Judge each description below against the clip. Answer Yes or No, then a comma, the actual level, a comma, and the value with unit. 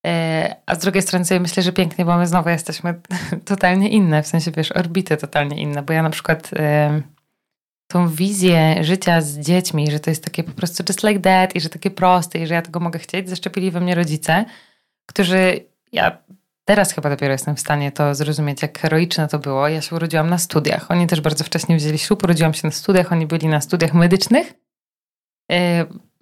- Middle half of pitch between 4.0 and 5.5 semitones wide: No, average, 2.9 semitones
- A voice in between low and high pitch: Yes, medium, 170 Hz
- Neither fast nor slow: No, fast, 200 wpm